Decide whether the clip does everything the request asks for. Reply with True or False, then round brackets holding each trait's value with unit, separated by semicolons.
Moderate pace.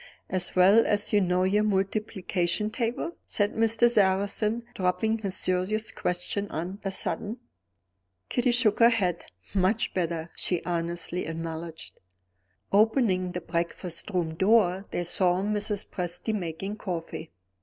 False (130 wpm)